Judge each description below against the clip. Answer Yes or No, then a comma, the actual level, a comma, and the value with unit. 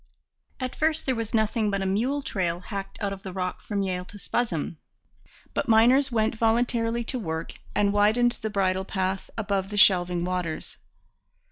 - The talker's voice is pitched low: No, high, 205 Hz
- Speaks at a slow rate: No, average, 170 wpm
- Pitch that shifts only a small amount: No, average, 3.5 semitones